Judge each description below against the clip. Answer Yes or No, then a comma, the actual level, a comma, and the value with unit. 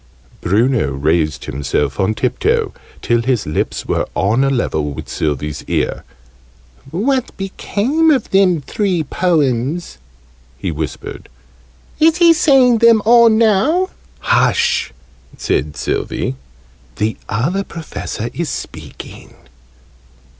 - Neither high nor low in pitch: Yes, medium, 150 Hz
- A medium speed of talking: No, slow, 110 wpm